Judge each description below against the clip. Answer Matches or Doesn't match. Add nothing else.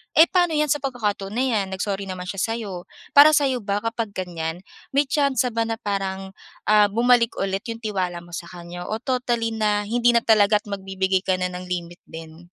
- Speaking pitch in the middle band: Doesn't match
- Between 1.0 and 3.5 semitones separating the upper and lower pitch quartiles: Doesn't match